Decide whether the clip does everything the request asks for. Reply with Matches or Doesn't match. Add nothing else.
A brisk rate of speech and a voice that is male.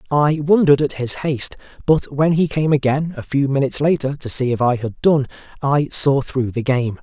Matches